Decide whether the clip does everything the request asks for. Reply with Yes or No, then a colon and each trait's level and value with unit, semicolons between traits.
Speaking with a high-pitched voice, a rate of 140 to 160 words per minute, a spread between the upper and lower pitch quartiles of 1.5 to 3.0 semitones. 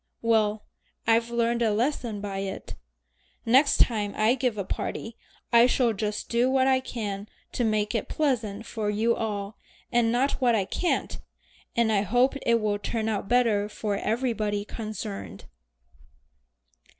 Yes: high, 225 Hz; average, 150 wpm; narrow, 2.4 semitones